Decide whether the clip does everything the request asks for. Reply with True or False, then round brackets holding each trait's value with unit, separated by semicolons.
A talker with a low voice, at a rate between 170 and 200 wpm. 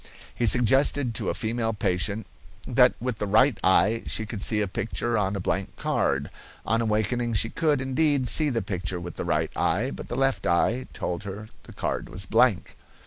True (110 Hz; 195 wpm)